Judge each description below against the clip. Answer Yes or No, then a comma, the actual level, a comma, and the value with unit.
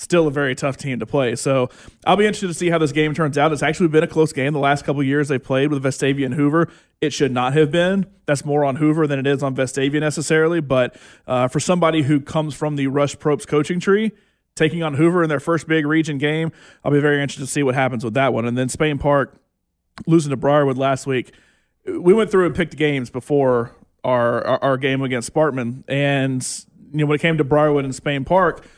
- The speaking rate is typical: No, fast, 240 wpm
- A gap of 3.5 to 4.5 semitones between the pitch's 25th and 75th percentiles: No, average, 2.7 semitones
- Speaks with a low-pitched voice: No, medium, 145 Hz